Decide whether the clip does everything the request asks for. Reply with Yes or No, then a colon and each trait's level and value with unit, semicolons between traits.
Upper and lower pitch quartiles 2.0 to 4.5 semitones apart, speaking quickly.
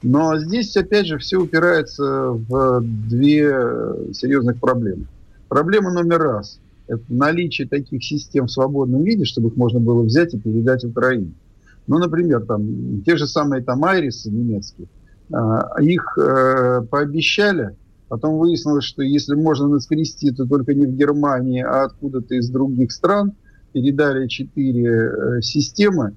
No: average, 4.1 semitones; average, 130 wpm